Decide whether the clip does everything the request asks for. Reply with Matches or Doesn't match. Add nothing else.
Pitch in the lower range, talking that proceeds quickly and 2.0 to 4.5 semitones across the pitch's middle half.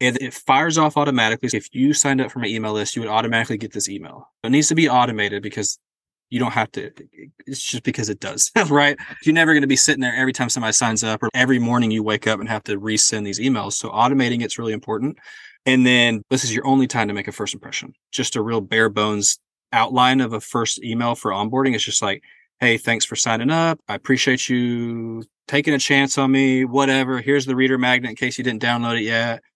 Matches